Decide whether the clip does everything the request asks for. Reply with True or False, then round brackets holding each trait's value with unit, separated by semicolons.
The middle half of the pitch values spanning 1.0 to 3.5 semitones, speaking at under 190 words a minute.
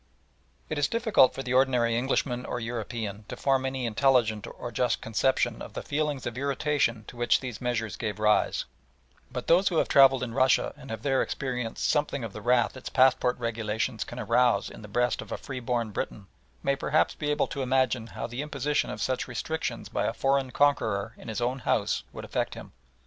False (2.8 semitones; 200 wpm)